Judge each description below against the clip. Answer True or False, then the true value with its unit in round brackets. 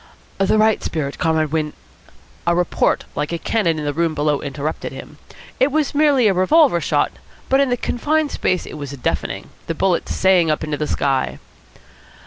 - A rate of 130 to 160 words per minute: False (185 wpm)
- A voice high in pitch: False (170 Hz)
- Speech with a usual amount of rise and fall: False (6.8 semitones)